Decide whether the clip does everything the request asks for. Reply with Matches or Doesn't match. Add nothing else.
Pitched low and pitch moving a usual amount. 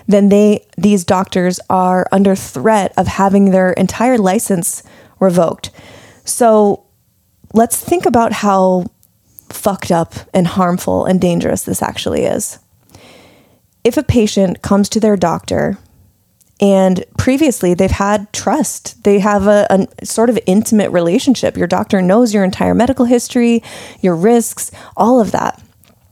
Doesn't match